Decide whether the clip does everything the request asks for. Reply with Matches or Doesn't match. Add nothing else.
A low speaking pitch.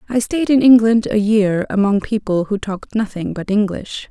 Doesn't match